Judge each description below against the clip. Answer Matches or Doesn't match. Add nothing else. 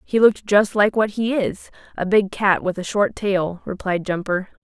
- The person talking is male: Doesn't match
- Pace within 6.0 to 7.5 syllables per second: Doesn't match